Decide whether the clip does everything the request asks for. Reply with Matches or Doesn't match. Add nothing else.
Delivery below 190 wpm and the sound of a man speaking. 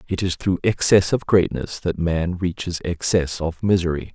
Matches